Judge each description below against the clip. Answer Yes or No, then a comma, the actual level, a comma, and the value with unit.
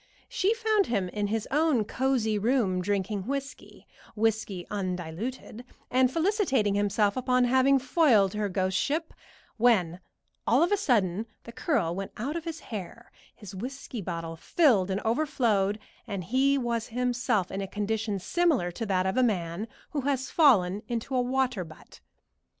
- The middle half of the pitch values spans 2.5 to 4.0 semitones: No, average, 5.2 semitones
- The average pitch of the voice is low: No, high, 225 Hz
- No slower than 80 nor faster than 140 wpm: No, average, 155 wpm